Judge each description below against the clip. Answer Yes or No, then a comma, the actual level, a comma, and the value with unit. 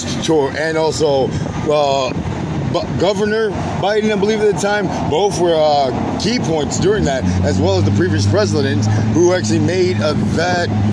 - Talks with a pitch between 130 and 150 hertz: Yes, medium, 140 Hz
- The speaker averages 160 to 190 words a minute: Yes, average, 165 wpm